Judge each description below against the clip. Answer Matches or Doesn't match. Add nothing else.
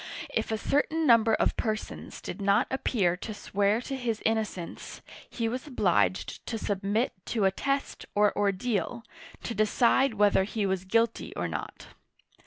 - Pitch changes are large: Doesn't match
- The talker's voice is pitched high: Matches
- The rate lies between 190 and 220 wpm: Doesn't match